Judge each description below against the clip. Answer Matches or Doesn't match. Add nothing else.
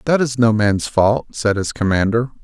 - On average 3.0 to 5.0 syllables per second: Matches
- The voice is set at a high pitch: Doesn't match